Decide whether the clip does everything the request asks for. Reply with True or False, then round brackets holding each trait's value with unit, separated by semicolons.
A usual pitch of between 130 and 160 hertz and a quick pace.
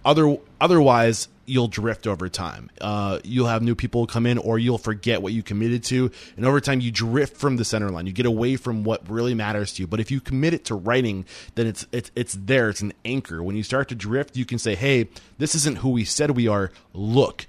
False (115 Hz; 240 wpm)